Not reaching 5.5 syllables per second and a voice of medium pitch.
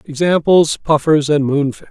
Yes: 4.7 syllables/s; medium, 150 Hz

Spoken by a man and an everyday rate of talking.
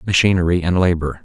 Yes: male; average, 145 wpm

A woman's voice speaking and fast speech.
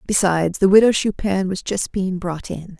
No: female; average, 195 wpm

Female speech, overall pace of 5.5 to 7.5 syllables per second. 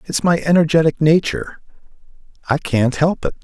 No: male; 6.0 syllables/s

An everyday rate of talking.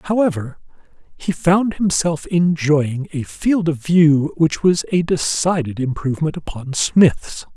No: slow, 125 wpm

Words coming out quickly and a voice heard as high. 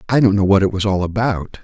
No: fast, 295 wpm; low, 100 Hz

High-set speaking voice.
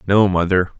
No: very low, 95 Hz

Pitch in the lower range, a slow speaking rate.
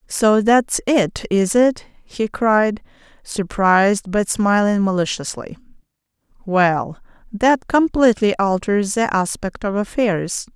No: high, 210 Hz; slow, 110 wpm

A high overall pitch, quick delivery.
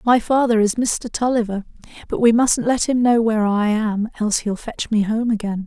Yes: high, 225 Hz; fast, 210 wpm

